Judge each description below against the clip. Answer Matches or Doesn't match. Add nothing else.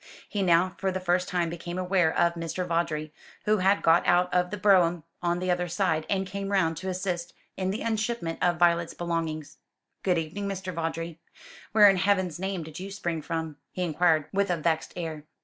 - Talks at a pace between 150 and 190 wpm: Doesn't match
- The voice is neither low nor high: Matches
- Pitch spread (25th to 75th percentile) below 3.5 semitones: Matches